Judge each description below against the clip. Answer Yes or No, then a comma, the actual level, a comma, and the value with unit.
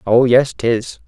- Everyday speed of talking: Yes, average, 165 wpm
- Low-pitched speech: Yes, low, 115 Hz